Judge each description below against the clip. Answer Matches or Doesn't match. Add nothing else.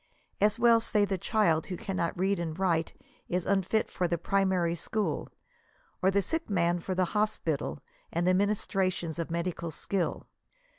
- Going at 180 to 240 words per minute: Doesn't match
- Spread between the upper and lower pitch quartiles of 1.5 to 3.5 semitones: Matches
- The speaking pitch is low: Doesn't match